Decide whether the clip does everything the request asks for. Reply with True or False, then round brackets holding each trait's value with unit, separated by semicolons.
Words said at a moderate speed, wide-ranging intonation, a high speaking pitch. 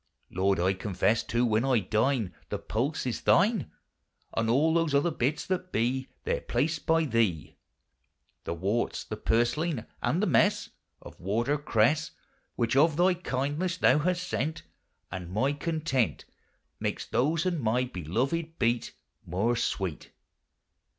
False (145 wpm; 6.4 semitones; 130 Hz)